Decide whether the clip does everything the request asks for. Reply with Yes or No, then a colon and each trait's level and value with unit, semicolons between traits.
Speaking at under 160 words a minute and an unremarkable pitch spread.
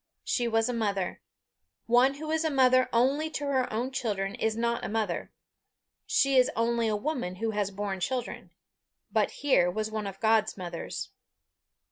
No: average, 165 wpm; average, 3.9 semitones